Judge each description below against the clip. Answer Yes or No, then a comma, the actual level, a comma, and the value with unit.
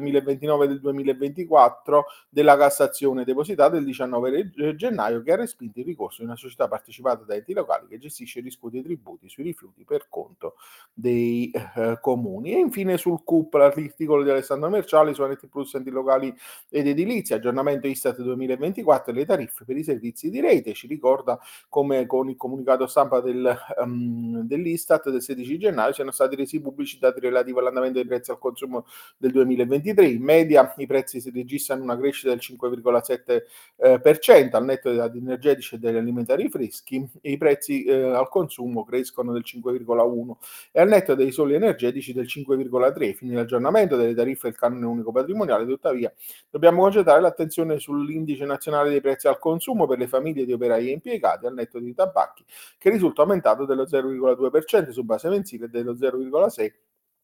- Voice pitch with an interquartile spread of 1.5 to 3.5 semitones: No, average, 3.9 semitones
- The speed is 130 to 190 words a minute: Yes, fast, 170 wpm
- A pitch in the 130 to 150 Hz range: Yes, low, 135 Hz